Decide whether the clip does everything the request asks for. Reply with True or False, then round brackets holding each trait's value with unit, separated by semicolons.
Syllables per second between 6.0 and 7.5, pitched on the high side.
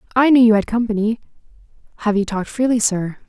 True (6.8 syllables/s; 220 Hz)